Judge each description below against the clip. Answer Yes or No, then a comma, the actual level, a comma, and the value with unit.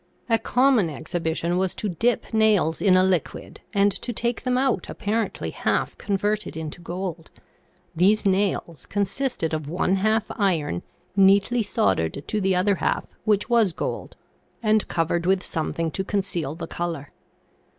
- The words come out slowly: No, average, 150 wpm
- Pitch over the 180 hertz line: Yes, high, 190 Hz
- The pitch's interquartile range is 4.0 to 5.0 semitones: Yes, average, 4.3 semitones